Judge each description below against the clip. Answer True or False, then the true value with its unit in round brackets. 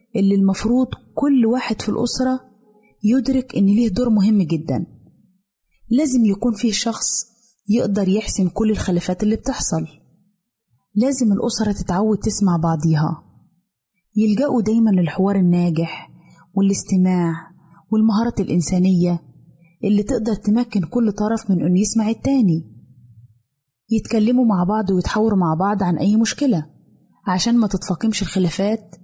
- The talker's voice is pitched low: False (205 Hz)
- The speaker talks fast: False (115 wpm)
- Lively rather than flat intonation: False (3.9 semitones)